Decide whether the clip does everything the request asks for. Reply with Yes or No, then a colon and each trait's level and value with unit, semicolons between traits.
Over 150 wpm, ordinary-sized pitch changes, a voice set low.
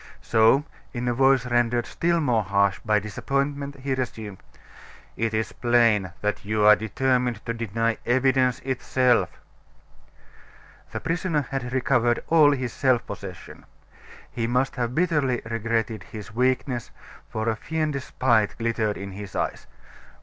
No: slow, 135 wpm; average, 3.2 semitones; low, 120 Hz